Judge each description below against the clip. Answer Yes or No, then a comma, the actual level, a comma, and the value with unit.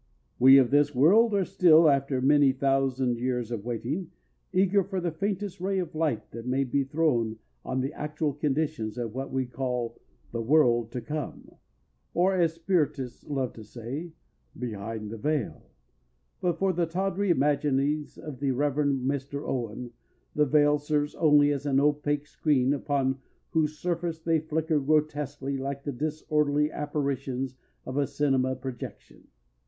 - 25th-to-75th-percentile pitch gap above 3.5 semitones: No, average, 3.1 semitones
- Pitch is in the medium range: Yes, medium, 145 Hz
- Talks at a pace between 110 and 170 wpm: Yes, average, 155 wpm